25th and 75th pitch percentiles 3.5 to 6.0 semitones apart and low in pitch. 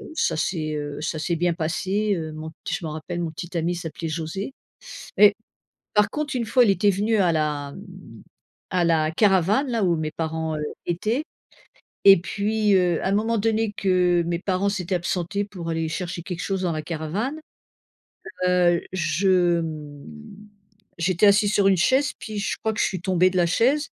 No: average, 3.9 semitones; medium, 180 Hz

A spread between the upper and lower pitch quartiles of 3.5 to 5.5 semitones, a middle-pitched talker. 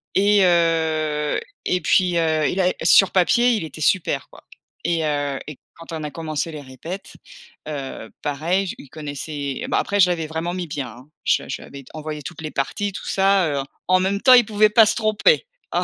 Yes: average, 4.2 semitones; medium, 165 Hz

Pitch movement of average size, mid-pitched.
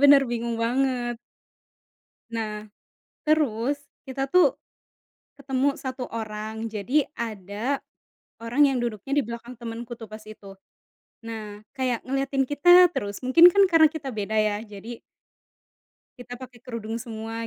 No: average, 3.7 semitones; high, 240 Hz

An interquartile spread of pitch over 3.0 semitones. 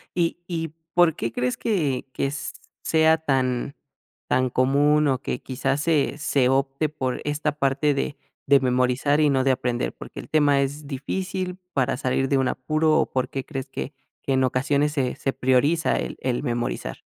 No: average, 2.7 semitones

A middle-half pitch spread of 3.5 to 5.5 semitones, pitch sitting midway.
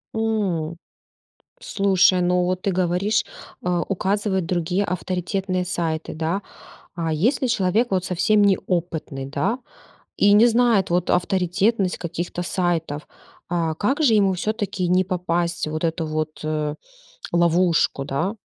No: average, 2.8 semitones; medium, 180 Hz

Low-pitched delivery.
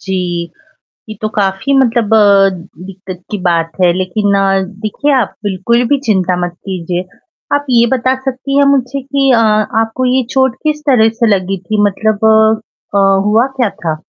No: high, 215 Hz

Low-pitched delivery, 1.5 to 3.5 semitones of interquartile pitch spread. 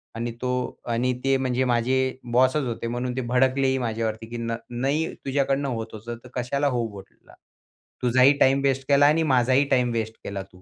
Yes: low, 125 Hz; narrow, 2.4 semitones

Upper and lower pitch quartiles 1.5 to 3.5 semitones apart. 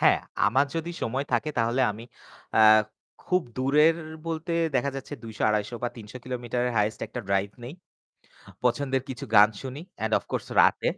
No: average, 4.0 semitones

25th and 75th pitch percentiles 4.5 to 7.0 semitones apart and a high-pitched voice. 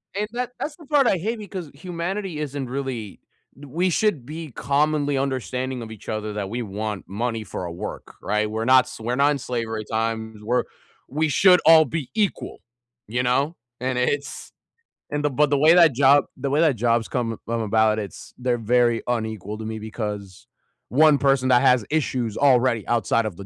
No: average, 5.1 semitones; low, 125 Hz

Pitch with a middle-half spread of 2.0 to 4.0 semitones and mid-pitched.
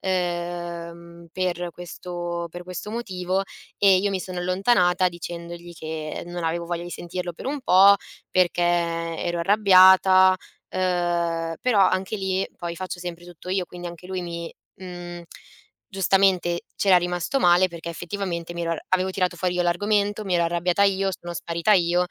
No: narrow, 1.5 semitones; medium, 175 Hz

